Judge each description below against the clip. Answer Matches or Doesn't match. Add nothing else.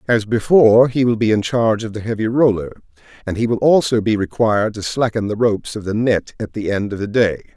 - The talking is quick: Matches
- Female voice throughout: Doesn't match